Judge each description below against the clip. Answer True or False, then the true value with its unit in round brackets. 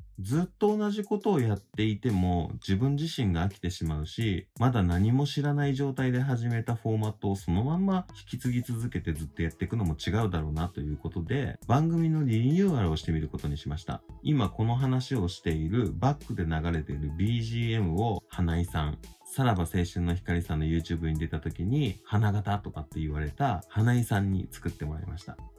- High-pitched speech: False (100 Hz)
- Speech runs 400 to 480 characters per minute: True (410 characters per minute)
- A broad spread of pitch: True (6.6 semitones)